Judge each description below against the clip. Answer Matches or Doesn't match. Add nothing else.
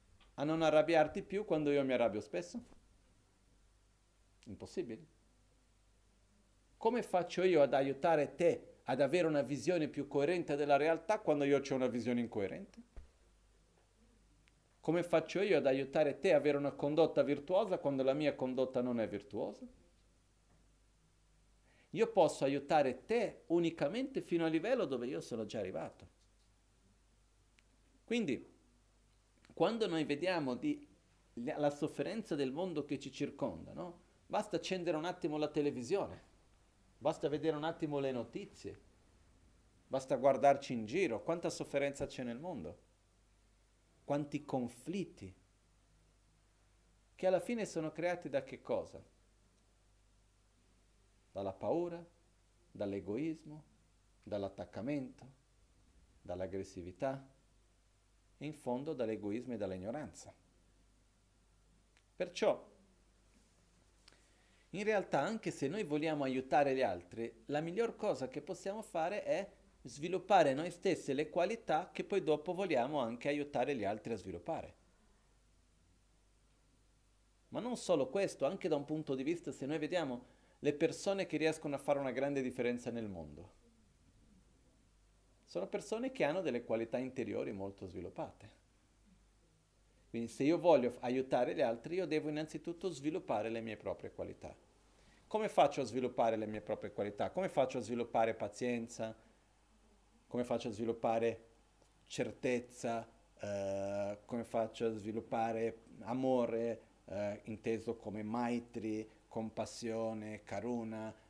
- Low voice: Matches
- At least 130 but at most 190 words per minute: Doesn't match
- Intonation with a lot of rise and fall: Matches